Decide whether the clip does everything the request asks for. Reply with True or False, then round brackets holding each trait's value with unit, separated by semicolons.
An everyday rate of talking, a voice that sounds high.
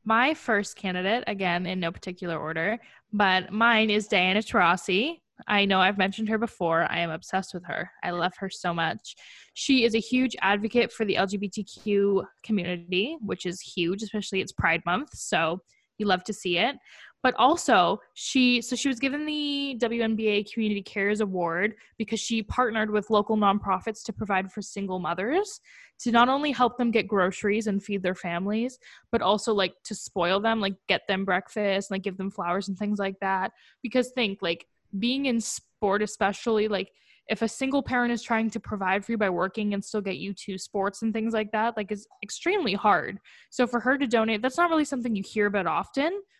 True (195 wpm; 210 Hz)